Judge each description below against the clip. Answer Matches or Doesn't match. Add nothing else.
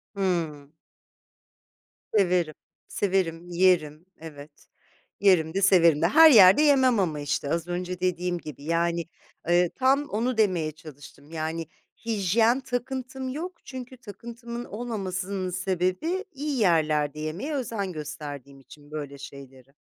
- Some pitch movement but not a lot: Doesn't match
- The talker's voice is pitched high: Doesn't match